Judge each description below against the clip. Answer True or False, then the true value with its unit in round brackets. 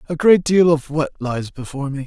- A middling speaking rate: False (230 wpm)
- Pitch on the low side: False (150 Hz)